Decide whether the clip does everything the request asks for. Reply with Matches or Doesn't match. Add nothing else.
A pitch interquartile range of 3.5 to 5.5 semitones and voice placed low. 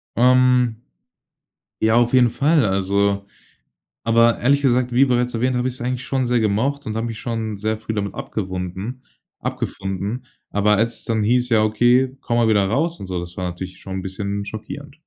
Matches